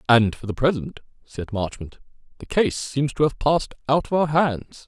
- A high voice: No, low, 135 Hz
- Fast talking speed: No, average, 195 wpm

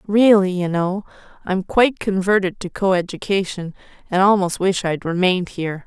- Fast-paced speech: No, average, 155 wpm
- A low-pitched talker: No, high, 190 Hz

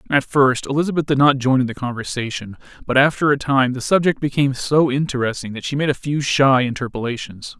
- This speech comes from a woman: No, male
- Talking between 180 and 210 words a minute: Yes, average, 195 wpm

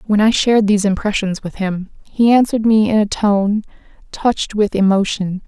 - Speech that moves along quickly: No, average, 175 wpm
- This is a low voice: No, high, 210 Hz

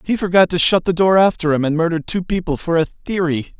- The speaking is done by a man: Yes, male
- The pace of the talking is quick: Yes, fast, 250 wpm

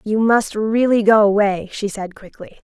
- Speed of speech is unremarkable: Yes, average, 175 wpm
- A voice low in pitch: No, high, 210 Hz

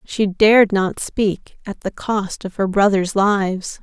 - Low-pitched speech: No, high, 200 Hz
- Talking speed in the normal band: Yes, average, 170 wpm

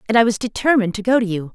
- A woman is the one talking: Yes, female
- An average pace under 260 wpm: No, fast, 310 wpm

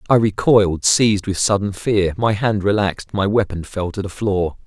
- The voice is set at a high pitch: No, low, 100 Hz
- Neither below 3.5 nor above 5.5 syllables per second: Yes, 5.0 syllables/s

